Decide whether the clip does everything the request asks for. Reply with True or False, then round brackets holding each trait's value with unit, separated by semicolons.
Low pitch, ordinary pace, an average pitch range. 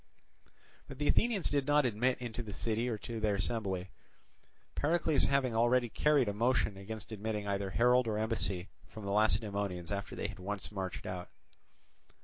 True (110 Hz; 165 wpm; 3.8 semitones)